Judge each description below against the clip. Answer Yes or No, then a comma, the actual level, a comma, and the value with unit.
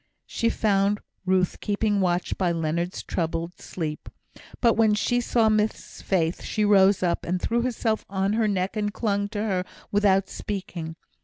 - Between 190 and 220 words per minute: No, average, 160 wpm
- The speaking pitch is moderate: No, high, 200 Hz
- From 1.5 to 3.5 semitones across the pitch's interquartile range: Yes, average, 2.9 semitones